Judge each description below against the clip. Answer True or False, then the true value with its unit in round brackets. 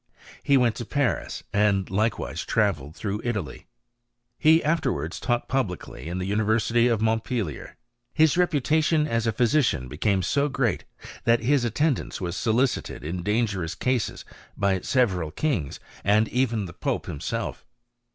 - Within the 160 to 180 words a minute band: False (145 wpm)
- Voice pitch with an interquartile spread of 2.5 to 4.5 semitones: False (5.1 semitones)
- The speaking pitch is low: True (115 Hz)